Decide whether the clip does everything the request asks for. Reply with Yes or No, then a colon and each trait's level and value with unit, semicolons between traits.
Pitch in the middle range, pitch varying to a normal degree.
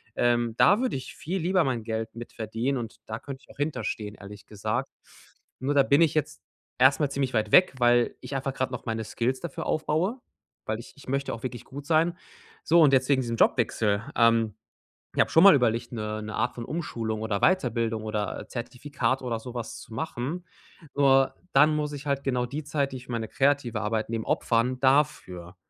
No: low, 125 Hz; average, 3.9 semitones